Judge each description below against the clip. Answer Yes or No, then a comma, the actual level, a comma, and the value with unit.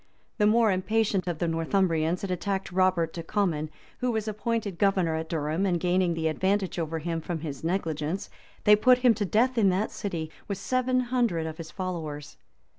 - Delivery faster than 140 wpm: Yes, average, 190 wpm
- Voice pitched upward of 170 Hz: Yes, medium, 185 Hz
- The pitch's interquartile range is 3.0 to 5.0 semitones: Yes, average, 4.3 semitones